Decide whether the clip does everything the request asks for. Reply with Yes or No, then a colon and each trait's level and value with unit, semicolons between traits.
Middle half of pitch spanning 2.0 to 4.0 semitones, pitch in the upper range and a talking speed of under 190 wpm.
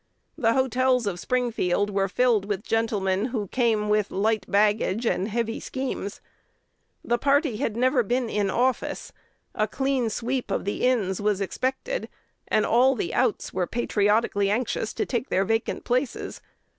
Yes: average, 3.6 semitones; high, 225 Hz; average, 155 wpm